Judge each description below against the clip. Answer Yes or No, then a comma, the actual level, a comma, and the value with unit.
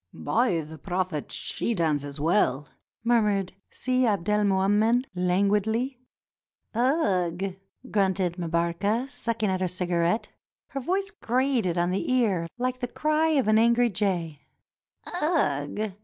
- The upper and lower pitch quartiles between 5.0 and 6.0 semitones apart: Yes, wide, 5.6 semitones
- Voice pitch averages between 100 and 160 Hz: No, high, 205 Hz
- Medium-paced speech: No, slow, 120 wpm